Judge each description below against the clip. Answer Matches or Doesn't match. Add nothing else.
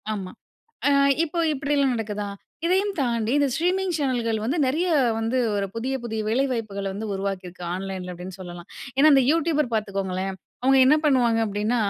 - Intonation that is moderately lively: Doesn't match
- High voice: Matches